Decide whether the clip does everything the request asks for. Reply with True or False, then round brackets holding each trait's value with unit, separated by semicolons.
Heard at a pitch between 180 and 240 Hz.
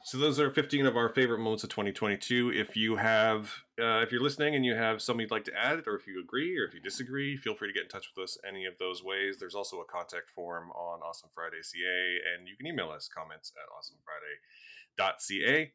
False (110 Hz)